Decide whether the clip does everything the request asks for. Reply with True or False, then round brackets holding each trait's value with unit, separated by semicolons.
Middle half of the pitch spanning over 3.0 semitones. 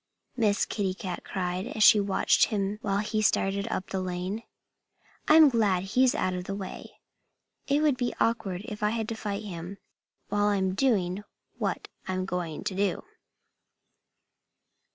False (2.7 semitones)